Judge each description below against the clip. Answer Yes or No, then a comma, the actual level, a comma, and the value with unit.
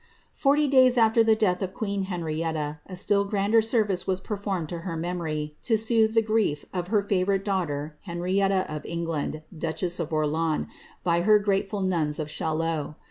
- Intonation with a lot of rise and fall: No, average, 4.3 semitones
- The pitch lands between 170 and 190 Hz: Yes, medium, 185 Hz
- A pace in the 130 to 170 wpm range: Yes, average, 160 wpm